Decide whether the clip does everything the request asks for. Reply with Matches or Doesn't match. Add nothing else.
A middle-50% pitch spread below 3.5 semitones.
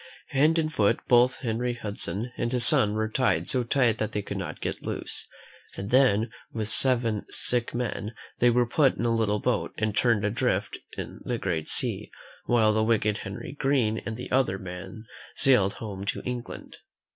Matches